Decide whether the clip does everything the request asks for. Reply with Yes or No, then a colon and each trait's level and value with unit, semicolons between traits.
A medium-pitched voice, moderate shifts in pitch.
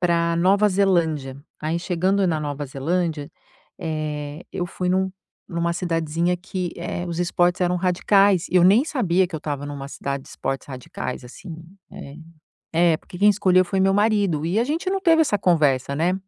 Yes: medium, 175 Hz; average, 3.6 semitones